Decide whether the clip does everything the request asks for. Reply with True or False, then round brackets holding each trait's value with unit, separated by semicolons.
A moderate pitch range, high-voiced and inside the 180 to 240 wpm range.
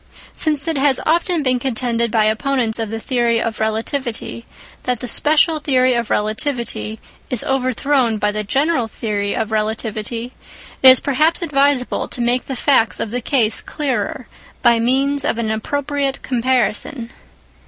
False (3.7 semitones; 250 Hz; 155 wpm)